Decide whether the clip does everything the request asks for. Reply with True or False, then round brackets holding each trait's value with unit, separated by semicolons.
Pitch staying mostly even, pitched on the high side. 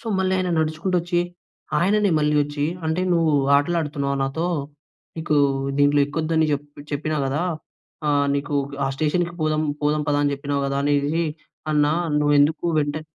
False (2.1 semitones; 150 Hz)